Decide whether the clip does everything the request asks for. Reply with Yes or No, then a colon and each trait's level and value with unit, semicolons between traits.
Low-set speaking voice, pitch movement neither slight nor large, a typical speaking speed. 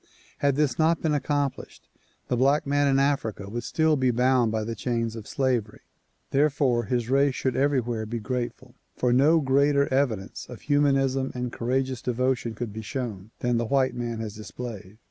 Yes: low, 125 Hz; average, 3.1 semitones; average, 175 wpm